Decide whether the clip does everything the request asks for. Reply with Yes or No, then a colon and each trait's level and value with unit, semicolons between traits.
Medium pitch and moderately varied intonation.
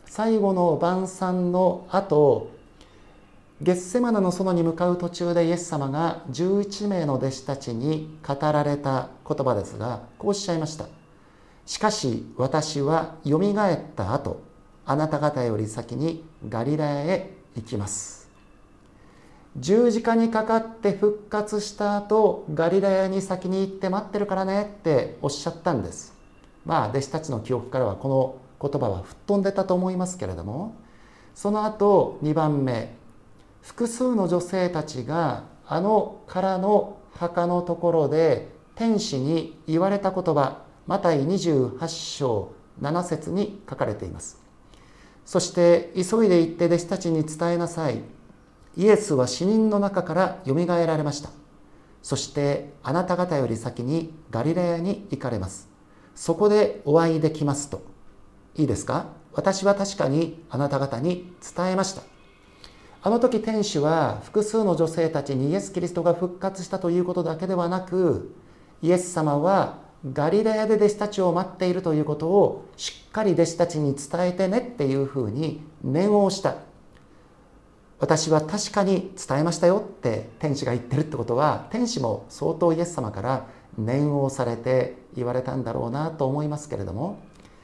No: medium, 165 Hz; wide, 5.7 semitones